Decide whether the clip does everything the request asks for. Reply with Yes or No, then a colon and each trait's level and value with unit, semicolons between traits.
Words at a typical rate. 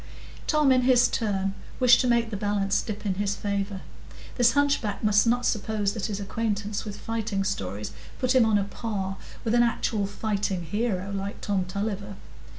Yes: average, 175 wpm